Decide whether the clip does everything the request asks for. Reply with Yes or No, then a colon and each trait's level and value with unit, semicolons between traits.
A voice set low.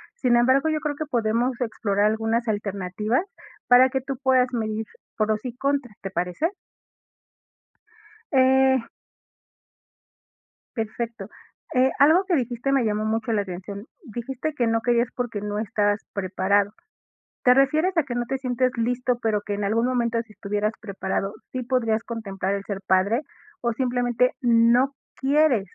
No: high, 235 Hz